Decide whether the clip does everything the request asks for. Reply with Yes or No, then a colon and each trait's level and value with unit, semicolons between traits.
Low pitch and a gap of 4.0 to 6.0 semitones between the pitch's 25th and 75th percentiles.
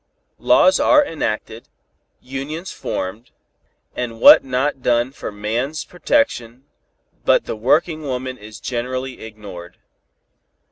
Yes: low, 125 Hz; average, 4.3 semitones